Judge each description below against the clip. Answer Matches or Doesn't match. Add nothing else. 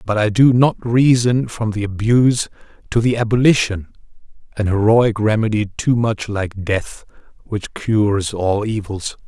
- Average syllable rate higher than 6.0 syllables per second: Doesn't match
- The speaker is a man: Matches